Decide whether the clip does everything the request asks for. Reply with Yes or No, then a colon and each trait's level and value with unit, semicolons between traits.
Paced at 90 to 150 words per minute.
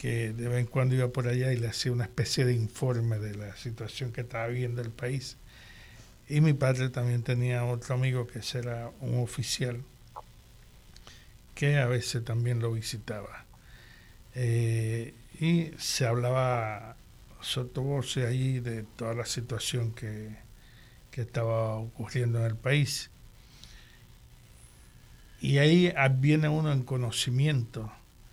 Yes: average, 140 wpm